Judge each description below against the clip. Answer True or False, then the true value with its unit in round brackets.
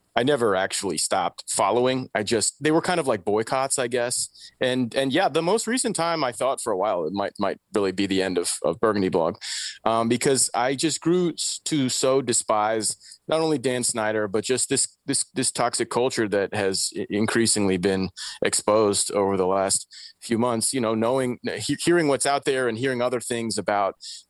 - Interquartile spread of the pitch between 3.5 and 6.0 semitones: True (4.3 semitones)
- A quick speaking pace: False (195 wpm)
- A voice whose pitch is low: True (120 Hz)